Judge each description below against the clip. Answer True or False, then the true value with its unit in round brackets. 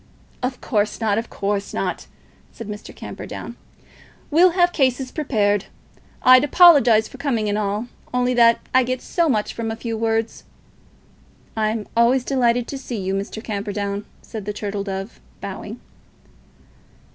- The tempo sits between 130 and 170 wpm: True (145 wpm)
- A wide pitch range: False (3.6 semitones)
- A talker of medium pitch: False (225 Hz)